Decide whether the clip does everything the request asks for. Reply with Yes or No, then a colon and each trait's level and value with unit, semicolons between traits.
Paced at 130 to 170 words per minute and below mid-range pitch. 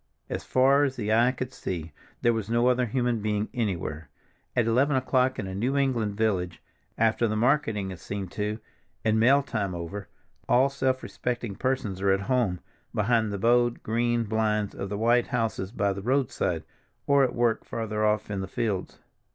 No: average, 185 wpm; low, 115 Hz